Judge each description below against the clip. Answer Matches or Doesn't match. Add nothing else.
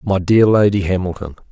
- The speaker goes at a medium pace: Matches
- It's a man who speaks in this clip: Matches